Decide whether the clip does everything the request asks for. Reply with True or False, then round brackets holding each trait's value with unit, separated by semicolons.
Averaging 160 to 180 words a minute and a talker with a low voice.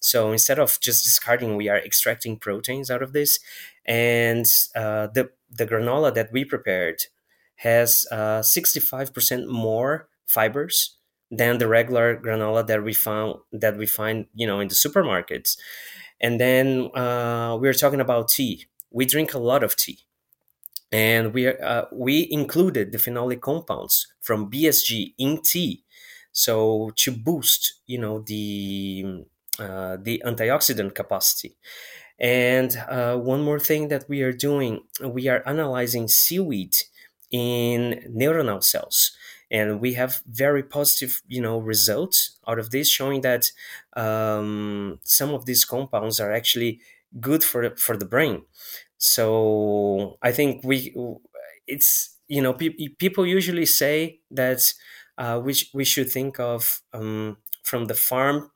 False (145 wpm; 120 Hz)